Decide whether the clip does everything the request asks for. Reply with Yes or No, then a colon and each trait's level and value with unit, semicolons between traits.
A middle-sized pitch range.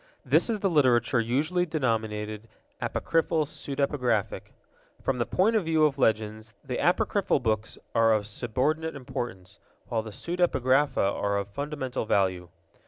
No: wide, 5.8 semitones